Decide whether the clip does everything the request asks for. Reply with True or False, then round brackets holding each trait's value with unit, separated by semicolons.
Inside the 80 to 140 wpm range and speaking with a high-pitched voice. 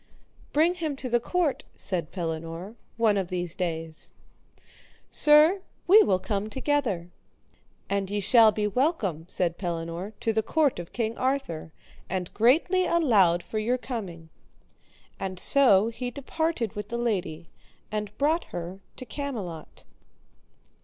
True (135 wpm; 215 Hz)